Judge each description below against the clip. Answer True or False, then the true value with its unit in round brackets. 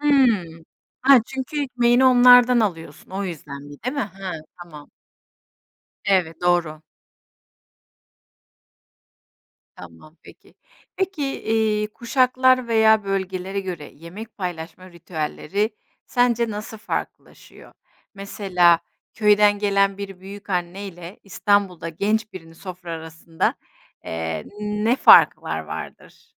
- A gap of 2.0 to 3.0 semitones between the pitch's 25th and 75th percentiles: False (4.6 semitones)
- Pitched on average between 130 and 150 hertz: False (200 Hz)